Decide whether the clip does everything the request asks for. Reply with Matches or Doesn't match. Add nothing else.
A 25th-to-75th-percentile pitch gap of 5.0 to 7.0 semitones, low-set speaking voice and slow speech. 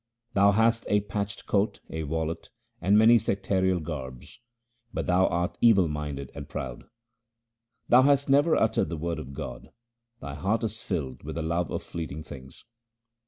Doesn't match